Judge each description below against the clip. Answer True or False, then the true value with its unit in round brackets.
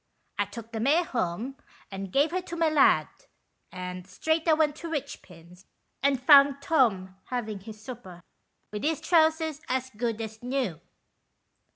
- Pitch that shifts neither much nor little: False (7.0 semitones)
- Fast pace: False (160 wpm)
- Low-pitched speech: False (255 Hz)